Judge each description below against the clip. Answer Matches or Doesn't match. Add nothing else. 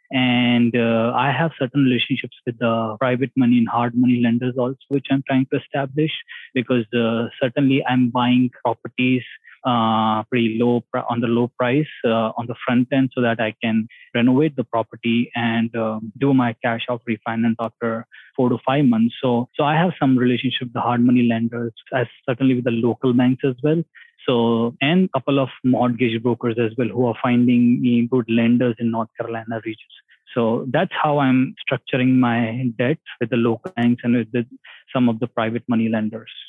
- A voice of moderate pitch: Doesn't match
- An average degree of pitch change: Doesn't match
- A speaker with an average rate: Matches